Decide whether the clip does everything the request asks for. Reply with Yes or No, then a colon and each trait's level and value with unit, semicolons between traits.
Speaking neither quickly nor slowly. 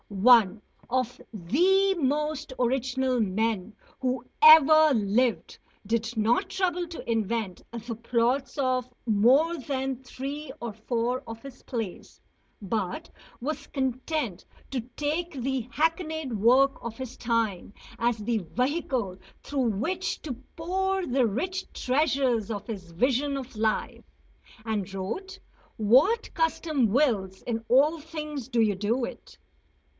No: slow, 125 wpm